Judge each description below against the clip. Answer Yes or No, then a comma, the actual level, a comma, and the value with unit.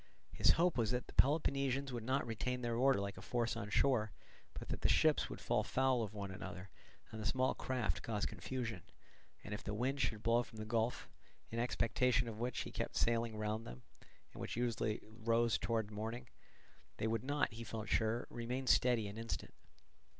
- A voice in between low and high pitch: No, low, 115 Hz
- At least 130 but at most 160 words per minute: No, average, 195 wpm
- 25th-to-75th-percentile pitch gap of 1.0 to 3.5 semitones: Yes, narrow, 2.6 semitones